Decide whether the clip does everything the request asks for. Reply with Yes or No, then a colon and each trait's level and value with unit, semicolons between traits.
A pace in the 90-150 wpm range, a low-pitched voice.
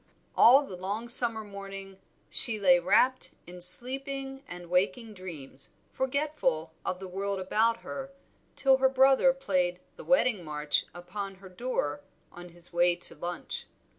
No: average, 145 wpm; high, 195 Hz